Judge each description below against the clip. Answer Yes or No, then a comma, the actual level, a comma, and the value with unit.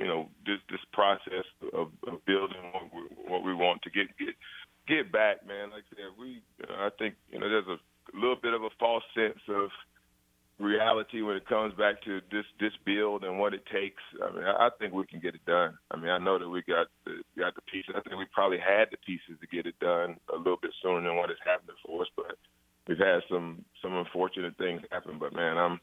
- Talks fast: Yes, fast, 240 wpm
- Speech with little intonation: No, average, 3.6 semitones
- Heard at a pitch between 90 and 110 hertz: Yes, very low, 95 Hz